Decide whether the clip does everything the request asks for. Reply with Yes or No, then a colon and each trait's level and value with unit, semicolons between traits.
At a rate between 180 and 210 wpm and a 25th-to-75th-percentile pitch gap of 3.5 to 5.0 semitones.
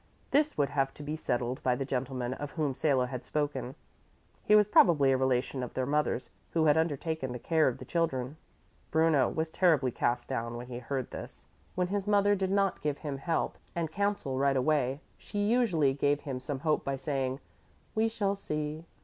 Yes: average, 195 wpm; average, 4.1 semitones